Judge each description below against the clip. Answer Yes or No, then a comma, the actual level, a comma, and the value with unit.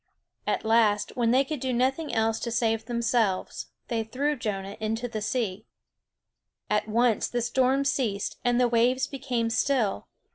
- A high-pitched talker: Yes, high, 235 Hz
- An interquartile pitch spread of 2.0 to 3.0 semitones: Yes, narrow, 2.5 semitones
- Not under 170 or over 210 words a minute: No, average, 155 wpm